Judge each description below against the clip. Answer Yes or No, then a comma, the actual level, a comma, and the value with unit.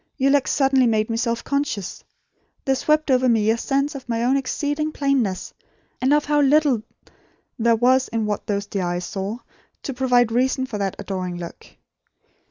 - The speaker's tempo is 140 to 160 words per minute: No, average, 180 wpm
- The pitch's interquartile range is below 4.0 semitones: No, average, 4.4 semitones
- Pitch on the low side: No, very high, 250 Hz